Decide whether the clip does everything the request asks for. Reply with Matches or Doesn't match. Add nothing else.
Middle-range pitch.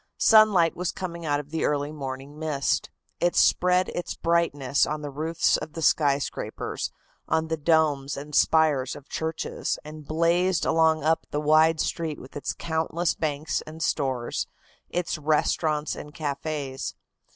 Matches